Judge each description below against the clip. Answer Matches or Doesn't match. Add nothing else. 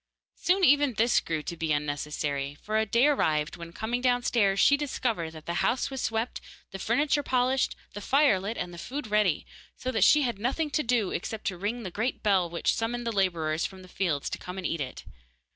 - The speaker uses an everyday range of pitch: Doesn't match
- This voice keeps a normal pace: Doesn't match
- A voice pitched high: Matches